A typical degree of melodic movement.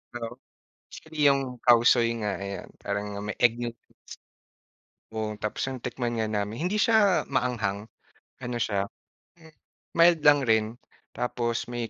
Yes: average, 3.9 semitones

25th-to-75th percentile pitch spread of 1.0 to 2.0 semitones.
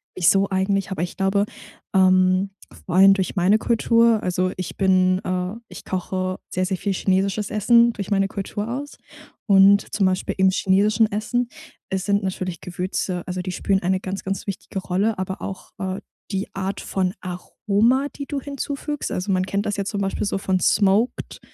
Yes: narrow, 1.7 semitones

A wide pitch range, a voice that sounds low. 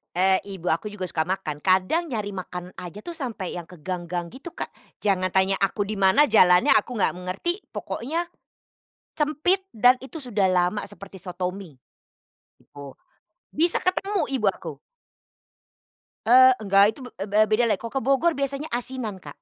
No: wide, 6.1 semitones; high, 205 Hz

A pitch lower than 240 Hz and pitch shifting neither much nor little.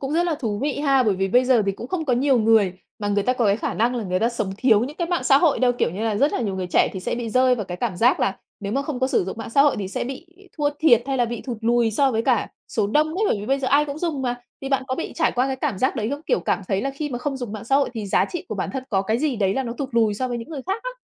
No: very high, 250 Hz; average, 4.2 semitones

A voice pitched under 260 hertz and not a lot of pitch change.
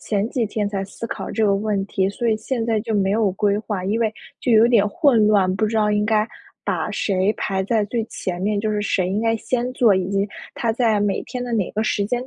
Yes: high, 210 Hz; narrow, 2.2 semitones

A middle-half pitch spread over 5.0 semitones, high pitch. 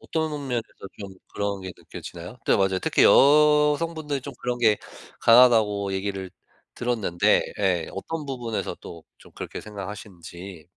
No: wide, 5.4 semitones; low, 105 Hz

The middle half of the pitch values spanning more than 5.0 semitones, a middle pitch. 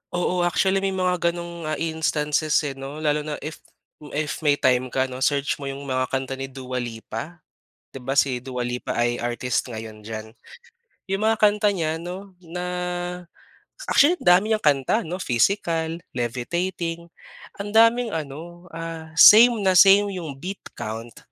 Yes: wide, 5.5 semitones; medium, 155 Hz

